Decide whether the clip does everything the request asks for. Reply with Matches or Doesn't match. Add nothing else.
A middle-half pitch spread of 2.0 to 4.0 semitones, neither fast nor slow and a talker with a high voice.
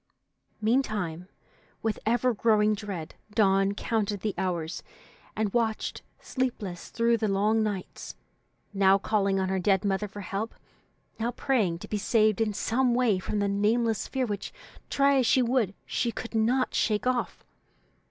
Matches